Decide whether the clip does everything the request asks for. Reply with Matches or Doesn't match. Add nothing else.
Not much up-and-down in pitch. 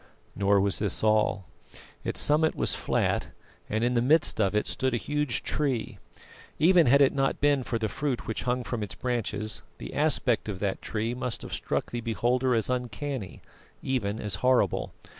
Doesn't match